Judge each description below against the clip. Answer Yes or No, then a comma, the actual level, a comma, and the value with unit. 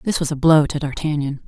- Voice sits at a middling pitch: Yes, medium, 150 Hz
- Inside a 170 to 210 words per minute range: No, fast, 245 wpm